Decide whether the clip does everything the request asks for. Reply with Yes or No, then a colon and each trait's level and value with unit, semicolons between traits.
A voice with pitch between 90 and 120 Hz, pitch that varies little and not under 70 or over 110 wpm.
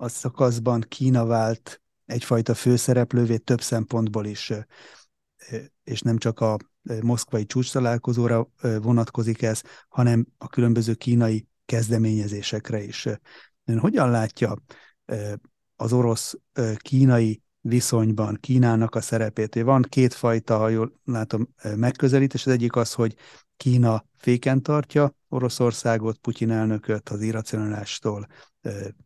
Yes: low, 115 Hz; narrow, 1.8 semitones; slow, 105 wpm